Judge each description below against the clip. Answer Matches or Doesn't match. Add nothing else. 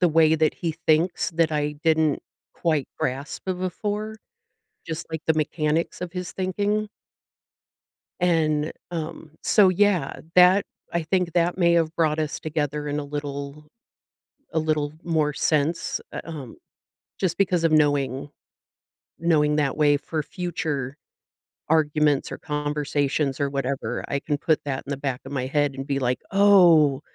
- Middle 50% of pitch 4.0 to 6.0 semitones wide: Doesn't match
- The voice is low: Doesn't match